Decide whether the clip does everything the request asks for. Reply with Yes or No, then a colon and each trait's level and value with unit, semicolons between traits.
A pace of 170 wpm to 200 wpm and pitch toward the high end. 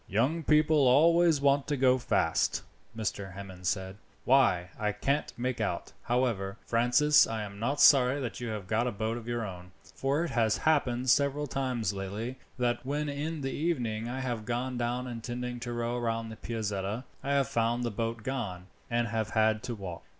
No: average, 190 wpm; low, 120 Hz